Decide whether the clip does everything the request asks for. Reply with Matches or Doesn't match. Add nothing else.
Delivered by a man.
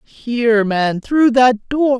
Doesn't match